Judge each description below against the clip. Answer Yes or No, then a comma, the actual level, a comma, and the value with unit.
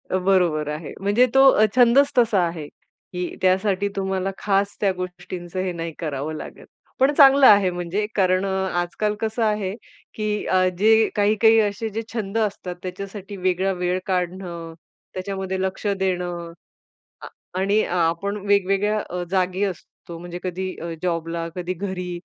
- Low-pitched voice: No, high, 190 Hz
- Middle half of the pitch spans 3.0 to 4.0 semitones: No, narrow, 2.6 semitones